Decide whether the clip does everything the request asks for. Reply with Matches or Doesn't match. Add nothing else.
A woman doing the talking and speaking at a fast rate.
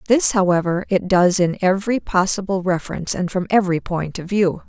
Doesn't match